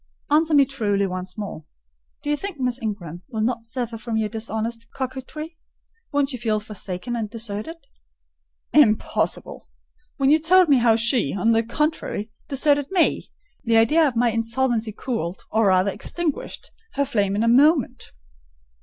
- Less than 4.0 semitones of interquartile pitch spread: No, average, 4.6 semitones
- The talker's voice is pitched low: No, high, 230 Hz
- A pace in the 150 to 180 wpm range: Yes, average, 155 wpm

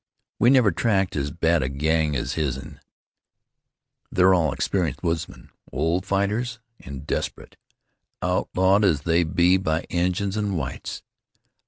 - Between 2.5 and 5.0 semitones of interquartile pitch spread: Yes, average, 4.0 semitones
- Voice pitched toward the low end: Yes, very low, 85 Hz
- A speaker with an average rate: No, slow, 130 wpm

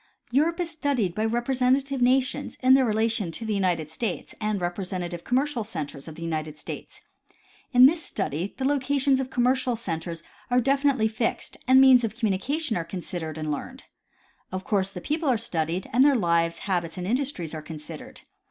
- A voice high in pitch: Yes, high, 220 Hz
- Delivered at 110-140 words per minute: No, average, 180 wpm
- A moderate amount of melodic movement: No, wide, 7.3 semitones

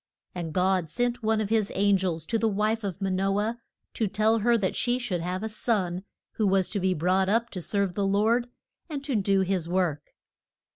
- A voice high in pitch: Yes, high, 200 Hz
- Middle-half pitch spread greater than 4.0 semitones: No, average, 3.2 semitones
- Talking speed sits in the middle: No, fast, 220 wpm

